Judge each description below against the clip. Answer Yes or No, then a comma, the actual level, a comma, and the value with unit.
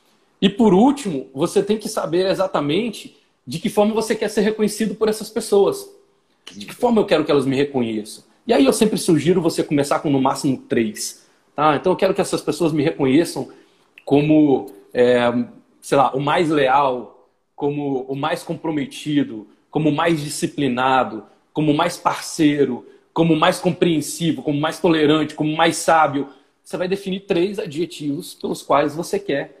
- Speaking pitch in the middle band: Yes, medium, 165 Hz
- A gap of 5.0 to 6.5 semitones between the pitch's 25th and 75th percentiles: Yes, wide, 5.6 semitones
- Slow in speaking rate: No, average, 170 wpm